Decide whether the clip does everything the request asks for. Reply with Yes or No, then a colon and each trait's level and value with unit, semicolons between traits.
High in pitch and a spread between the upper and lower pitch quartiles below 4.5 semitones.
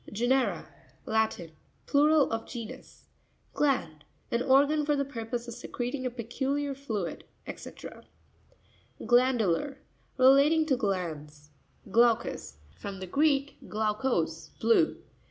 No: high, 240 Hz; average, 5.3 semitones